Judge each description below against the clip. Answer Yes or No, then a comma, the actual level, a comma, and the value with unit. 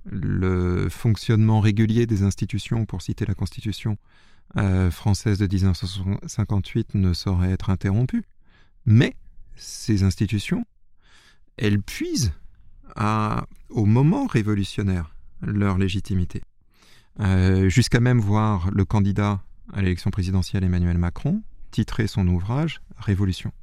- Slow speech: Yes, slow, 110 wpm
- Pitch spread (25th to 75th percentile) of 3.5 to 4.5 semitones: No, narrow, 2.6 semitones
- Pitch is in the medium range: No, low, 100 Hz